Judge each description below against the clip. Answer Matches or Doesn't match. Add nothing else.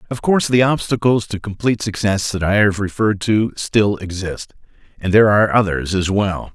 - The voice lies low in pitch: Matches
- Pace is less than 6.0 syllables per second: Matches